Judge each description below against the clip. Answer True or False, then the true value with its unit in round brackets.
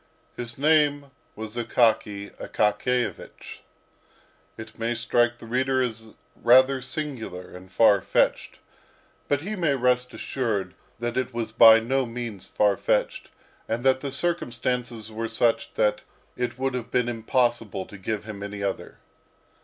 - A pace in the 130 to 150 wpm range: True (140 wpm)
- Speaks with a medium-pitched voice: False (120 Hz)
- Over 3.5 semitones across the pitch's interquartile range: False (2.8 semitones)